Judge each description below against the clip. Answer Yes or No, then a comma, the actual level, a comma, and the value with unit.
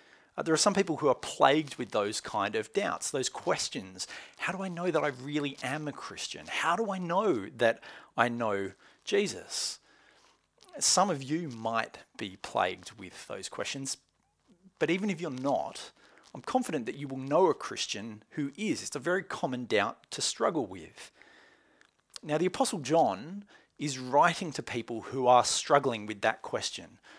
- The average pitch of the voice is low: No, medium, 150 Hz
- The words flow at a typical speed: Yes, average, 170 wpm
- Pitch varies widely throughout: Yes, wide, 6.1 semitones